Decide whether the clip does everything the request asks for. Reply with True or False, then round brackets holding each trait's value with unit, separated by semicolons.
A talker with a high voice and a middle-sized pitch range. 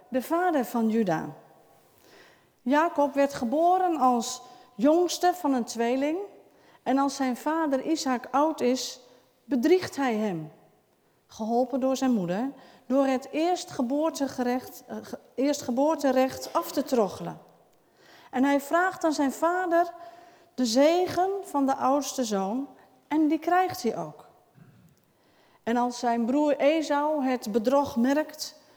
True (275 Hz; 4.1 semitones)